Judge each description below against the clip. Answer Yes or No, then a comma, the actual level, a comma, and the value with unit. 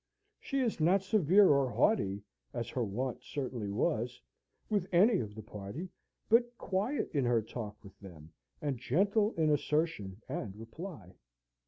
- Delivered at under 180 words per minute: Yes, average, 150 wpm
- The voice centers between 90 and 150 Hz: Yes, medium, 140 Hz